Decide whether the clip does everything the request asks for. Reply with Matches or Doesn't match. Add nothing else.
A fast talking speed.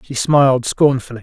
Doesn't match